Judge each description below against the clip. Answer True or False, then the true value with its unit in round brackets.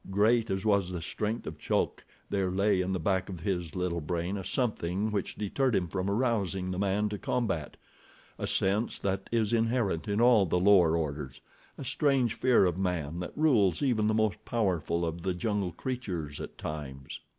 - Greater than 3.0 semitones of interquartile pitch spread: True (3.8 semitones)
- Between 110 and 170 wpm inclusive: False (185 wpm)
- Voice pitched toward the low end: True (95 Hz)